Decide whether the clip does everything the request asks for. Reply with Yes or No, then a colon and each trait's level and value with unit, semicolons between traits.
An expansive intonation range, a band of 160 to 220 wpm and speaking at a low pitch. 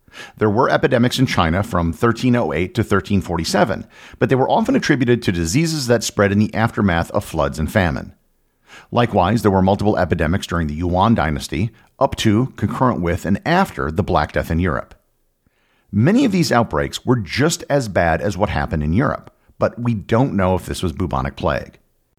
Yes: wide, 6.0 semitones; average, 180 wpm; low, 100 Hz